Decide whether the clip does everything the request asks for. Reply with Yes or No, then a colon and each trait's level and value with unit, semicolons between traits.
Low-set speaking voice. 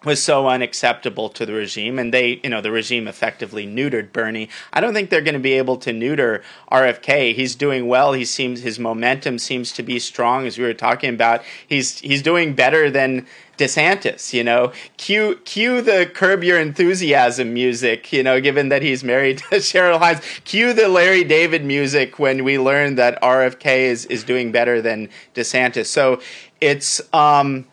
Yes: low, 130 Hz